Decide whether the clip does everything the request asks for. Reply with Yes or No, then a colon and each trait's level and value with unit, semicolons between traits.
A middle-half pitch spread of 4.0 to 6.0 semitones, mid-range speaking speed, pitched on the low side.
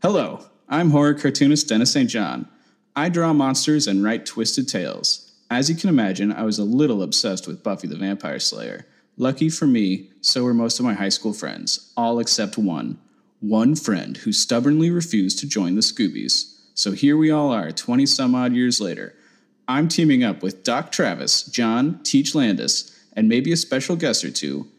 Yes: wide, 5.5 semitones; average, 185 wpm; low, 130 Hz